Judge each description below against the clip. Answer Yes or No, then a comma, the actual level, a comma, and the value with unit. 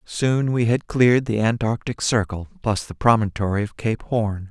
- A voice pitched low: Yes, low, 110 Hz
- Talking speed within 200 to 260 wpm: No, average, 175 wpm